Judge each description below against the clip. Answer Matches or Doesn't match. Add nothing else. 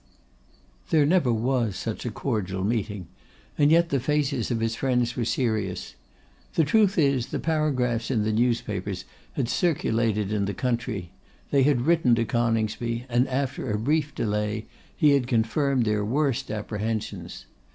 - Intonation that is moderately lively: Matches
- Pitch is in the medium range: Doesn't match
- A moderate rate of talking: Matches